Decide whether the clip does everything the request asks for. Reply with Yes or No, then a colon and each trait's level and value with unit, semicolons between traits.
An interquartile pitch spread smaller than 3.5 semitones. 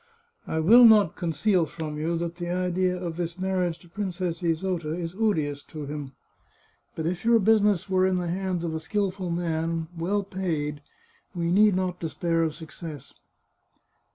Yes: narrow, 2.6 semitones